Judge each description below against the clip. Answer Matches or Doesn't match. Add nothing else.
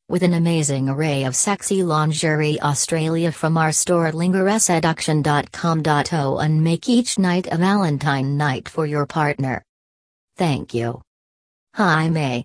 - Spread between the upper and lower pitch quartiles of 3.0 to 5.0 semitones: Matches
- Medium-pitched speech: Matches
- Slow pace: Matches